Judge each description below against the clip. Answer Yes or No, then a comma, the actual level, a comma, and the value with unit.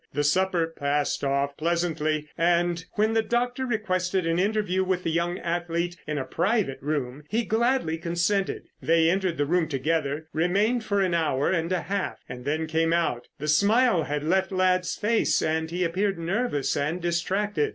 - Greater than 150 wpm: Yes, average, 170 wpm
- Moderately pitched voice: Yes, medium, 170 Hz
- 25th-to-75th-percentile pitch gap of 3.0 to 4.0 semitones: Yes, average, 3.5 semitones